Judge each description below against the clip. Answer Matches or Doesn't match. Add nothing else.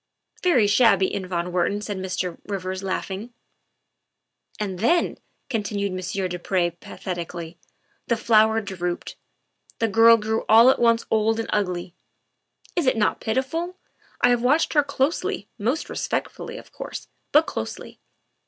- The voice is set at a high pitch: Matches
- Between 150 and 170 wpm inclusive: Matches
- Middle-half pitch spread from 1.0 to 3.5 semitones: Doesn't match